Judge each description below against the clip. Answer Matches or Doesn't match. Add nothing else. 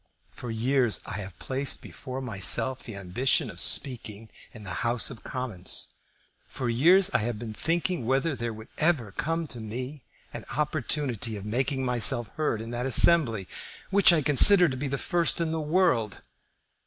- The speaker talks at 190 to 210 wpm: Doesn't match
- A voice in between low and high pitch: Doesn't match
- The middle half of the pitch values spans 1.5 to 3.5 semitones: Doesn't match